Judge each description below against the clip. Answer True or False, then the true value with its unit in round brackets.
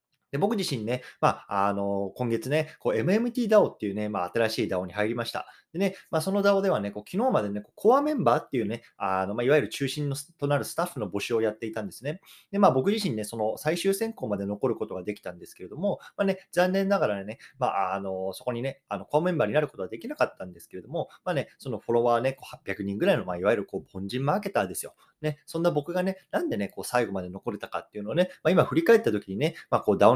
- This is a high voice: False (135 Hz)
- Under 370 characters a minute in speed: False (495 characters per minute)